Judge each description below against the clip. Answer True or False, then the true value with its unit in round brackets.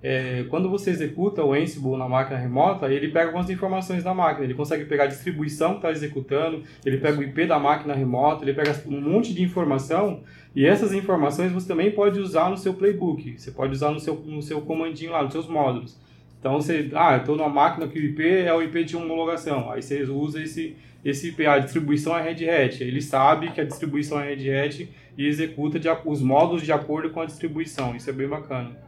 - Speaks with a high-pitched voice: False (155 Hz)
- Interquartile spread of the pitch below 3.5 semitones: True (2.8 semitones)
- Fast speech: True (215 wpm)